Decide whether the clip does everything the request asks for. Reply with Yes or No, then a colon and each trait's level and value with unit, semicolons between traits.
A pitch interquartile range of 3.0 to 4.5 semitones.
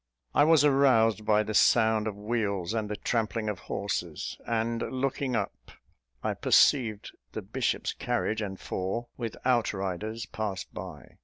No: narrow, 2.5 semitones